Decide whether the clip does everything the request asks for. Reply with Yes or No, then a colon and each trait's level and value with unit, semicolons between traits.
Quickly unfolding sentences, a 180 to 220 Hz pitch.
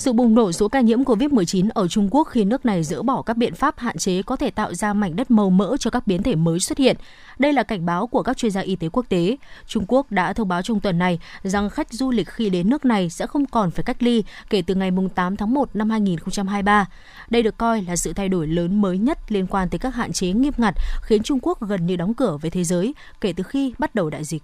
Yes: fast, 275 wpm; high, 210 Hz